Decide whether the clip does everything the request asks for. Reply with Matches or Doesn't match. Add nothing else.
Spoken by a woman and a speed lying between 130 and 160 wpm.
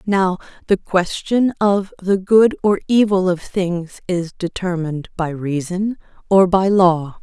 Matches